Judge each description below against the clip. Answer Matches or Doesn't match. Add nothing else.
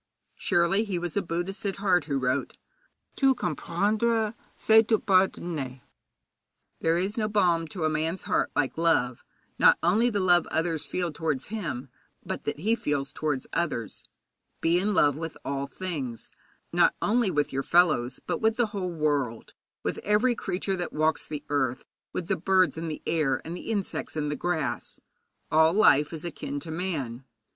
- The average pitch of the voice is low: Doesn't match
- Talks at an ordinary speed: Matches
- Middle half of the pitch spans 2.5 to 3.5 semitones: Doesn't match